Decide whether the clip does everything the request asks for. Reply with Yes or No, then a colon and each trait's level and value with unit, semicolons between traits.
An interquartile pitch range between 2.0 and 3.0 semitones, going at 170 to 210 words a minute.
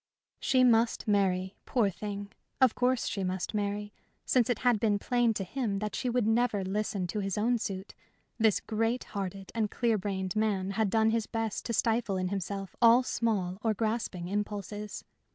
Yes: average, 2.7 semitones; average, 180 wpm